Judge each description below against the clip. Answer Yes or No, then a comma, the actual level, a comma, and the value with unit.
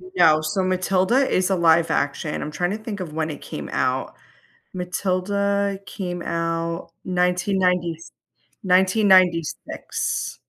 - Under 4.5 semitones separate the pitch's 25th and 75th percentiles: Yes, narrow, 2.4 semitones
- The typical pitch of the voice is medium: Yes, medium, 180 Hz